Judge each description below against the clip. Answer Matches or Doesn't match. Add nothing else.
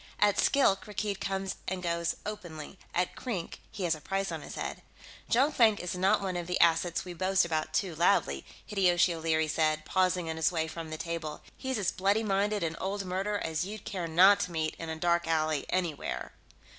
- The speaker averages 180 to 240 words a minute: Matches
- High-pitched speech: Doesn't match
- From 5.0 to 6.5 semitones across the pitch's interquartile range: Doesn't match